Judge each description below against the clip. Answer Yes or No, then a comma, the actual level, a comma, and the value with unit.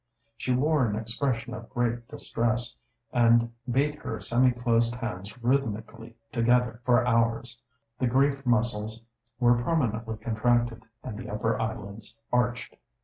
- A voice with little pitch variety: Yes, narrow, 1.5 semitones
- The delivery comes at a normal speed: No, slow, 130 wpm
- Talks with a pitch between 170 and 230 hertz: No, low, 120 Hz